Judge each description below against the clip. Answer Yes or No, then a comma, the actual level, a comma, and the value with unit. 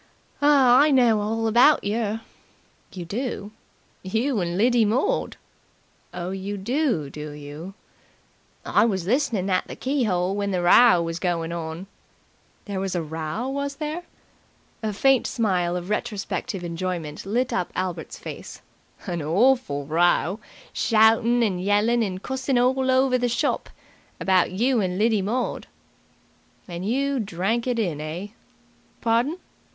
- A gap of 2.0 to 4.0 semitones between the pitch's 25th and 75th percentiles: No, wide, 5.6 semitones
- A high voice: Yes, high, 205 Hz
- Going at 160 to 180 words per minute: No, average, 140 wpm